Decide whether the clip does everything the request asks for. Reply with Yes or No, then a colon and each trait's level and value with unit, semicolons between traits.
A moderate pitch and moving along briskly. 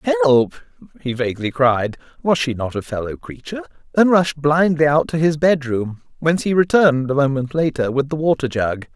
No: medium, 145 Hz; average, 170 wpm